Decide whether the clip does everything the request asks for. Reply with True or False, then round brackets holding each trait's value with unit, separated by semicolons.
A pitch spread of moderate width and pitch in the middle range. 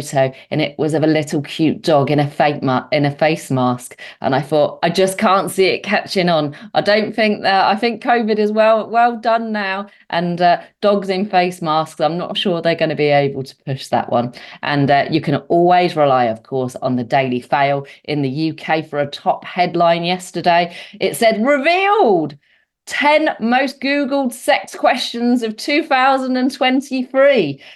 False (7.5 semitones; 175 Hz)